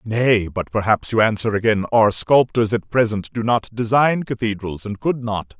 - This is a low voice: Yes, low, 110 Hz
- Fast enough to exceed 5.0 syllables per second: No, 4.7 syllables/s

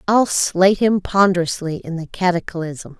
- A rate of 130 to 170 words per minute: Yes, average, 140 wpm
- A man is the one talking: No, female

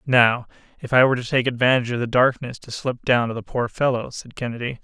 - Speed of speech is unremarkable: No, fast, 235 wpm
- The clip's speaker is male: Yes, male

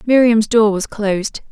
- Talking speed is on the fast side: No, average, 160 wpm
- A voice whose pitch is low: No, high, 220 Hz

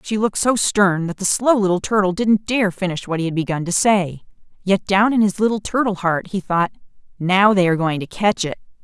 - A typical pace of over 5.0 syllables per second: Yes, 5.5 syllables/s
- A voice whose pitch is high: Yes, high, 195 Hz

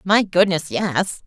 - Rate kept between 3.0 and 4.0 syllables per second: Yes, 3.5 syllables/s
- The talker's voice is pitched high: No, medium, 180 Hz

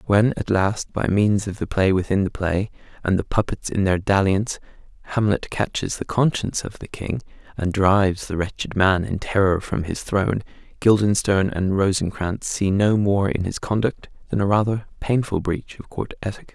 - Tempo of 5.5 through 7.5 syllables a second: No, 5.1 syllables/s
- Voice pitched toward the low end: Yes, low, 100 Hz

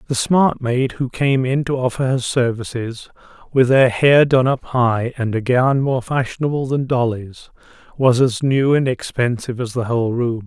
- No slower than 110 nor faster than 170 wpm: No, average, 185 wpm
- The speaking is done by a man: Yes, male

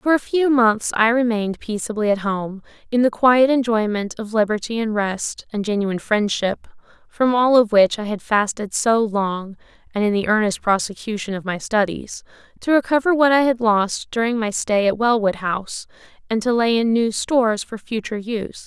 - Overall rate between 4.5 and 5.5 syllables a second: Yes, 5.0 syllables/s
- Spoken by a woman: Yes, female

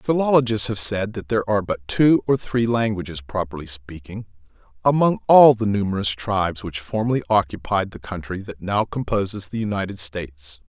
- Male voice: Yes, male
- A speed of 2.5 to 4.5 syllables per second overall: No, 5.4 syllables/s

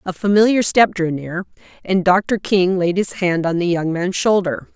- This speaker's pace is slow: No, average, 200 wpm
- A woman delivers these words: Yes, female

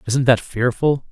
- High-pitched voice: No, low, 125 Hz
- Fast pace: No, average, 160 wpm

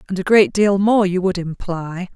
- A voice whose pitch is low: No, medium, 185 Hz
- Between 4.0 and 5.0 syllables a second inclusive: Yes, 4.7 syllables/s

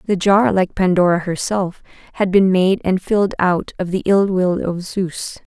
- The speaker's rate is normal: Yes, average, 185 wpm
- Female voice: Yes, female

